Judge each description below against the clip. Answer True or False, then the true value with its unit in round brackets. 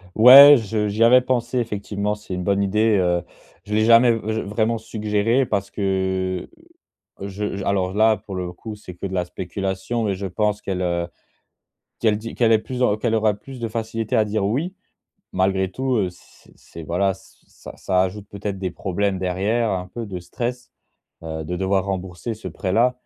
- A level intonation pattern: False (3.2 semitones)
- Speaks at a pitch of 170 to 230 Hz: False (105 Hz)